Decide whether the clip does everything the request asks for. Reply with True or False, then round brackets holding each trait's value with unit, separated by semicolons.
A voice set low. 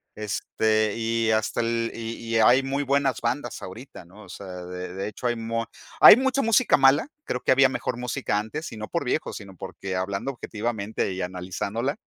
True (115 Hz)